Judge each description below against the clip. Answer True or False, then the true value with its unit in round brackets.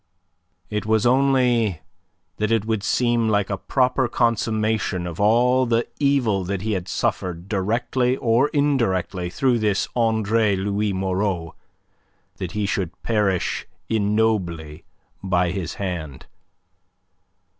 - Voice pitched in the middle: False (105 Hz)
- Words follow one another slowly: True (120 wpm)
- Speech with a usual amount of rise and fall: True (3.7 semitones)